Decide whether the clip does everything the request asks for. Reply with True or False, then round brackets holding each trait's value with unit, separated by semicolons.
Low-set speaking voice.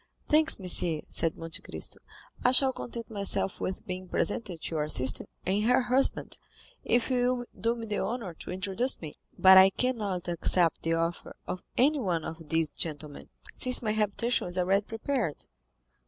False (195 Hz)